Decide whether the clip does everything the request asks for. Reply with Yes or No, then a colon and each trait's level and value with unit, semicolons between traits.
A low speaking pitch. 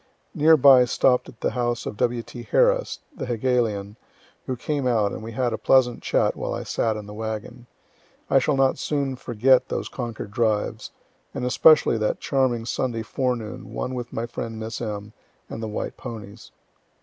Yes: low, 120 Hz